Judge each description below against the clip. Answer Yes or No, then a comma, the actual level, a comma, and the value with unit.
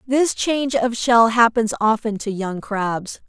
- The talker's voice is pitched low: No, high, 230 Hz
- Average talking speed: Yes, average, 165 wpm